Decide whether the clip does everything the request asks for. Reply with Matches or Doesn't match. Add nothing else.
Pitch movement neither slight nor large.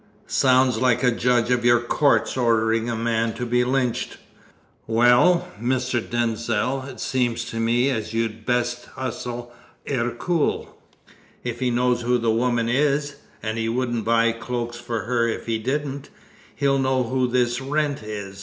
Doesn't match